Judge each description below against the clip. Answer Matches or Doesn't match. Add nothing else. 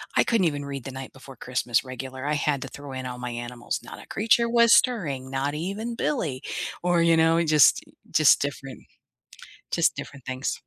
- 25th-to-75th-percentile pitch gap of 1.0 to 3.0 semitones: Doesn't match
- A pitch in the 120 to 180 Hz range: Matches